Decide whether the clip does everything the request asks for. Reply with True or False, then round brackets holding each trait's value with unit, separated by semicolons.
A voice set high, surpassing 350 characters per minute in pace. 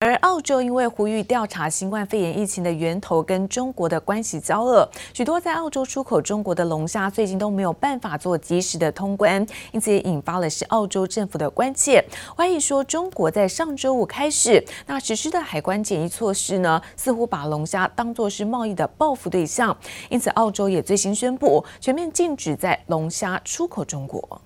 False (210 Hz; 300 characters per minute)